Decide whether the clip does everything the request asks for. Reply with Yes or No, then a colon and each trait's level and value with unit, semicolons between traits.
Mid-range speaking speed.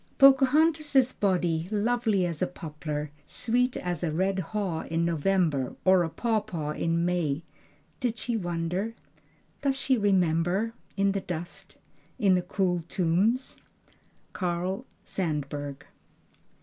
No: slow, 120 wpm